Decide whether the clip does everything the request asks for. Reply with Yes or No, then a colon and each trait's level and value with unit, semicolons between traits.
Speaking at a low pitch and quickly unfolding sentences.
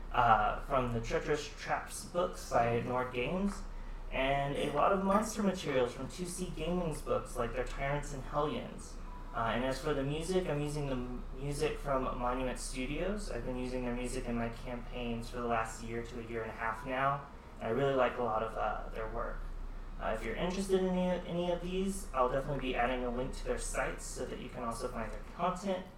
Yes: low, 130 Hz; fast, 215 wpm